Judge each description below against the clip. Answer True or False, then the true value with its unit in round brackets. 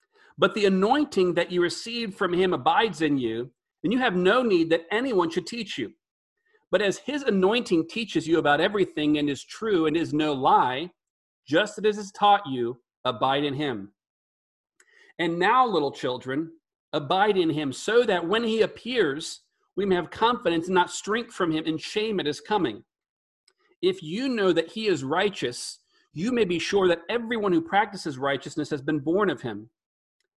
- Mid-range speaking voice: True (180 Hz)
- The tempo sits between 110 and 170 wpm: False (180 wpm)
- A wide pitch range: True (6.3 semitones)